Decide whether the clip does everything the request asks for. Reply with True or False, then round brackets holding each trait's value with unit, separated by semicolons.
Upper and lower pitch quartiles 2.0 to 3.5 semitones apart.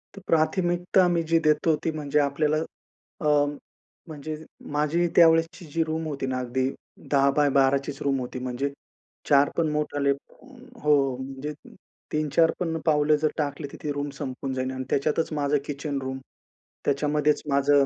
True (2.4 semitones)